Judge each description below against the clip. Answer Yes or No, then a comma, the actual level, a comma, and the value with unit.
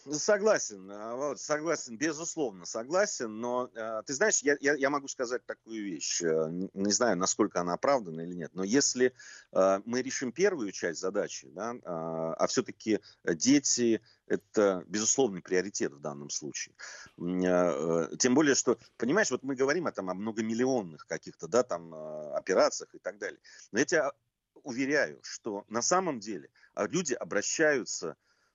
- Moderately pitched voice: No, low, 115 Hz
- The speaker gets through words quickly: No, average, 135 wpm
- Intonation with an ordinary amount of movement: No, wide, 7.8 semitones